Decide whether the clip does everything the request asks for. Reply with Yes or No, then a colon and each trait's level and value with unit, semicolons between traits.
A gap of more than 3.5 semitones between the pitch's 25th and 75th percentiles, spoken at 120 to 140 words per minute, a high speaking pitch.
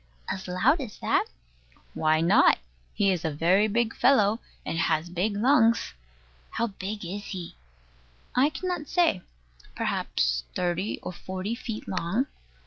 Yes: average, 4.9 semitones; slow, 135 wpm; high, 200 Hz